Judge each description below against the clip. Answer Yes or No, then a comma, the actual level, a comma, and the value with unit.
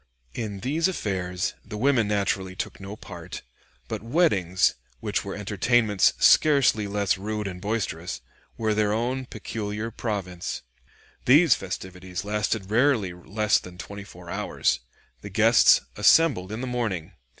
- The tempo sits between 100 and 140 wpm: Yes, slow, 135 wpm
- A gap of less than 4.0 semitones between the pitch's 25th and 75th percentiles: Yes, average, 3.6 semitones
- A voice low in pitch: Yes, low, 105 Hz